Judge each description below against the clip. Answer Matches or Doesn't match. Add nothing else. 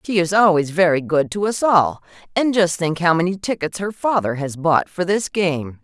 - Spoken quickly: Matches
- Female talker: Matches